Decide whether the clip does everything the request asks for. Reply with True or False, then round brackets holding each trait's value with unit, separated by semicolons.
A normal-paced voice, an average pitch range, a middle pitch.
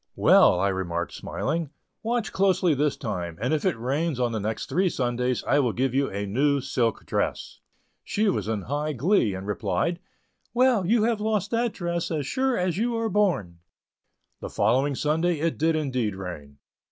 False (180 wpm; 8.5 semitones; 145 Hz)